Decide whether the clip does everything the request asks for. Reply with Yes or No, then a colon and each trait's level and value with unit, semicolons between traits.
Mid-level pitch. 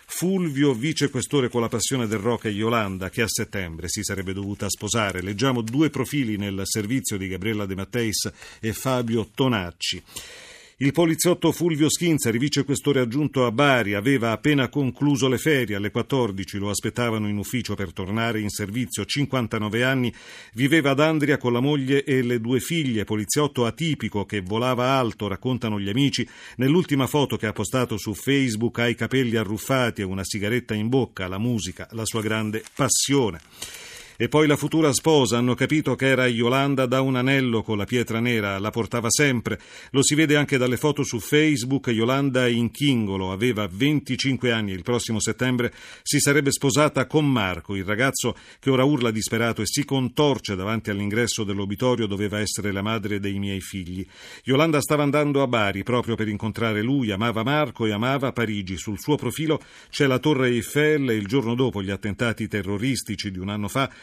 No: low, 120 Hz